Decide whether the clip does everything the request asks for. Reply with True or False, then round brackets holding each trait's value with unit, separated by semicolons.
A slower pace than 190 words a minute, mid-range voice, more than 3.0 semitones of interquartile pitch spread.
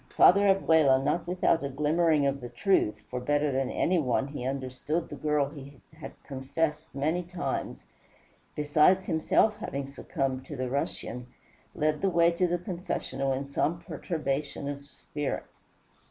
True (155 wpm; 145 Hz; 3.6 semitones)